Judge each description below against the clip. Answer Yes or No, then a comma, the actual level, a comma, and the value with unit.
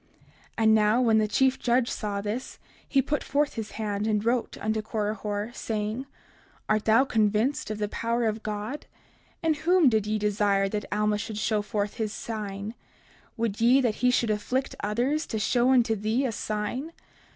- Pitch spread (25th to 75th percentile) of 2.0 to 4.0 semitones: Yes, average, 2.8 semitones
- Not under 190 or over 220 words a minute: No, average, 180 wpm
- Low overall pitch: No, high, 220 Hz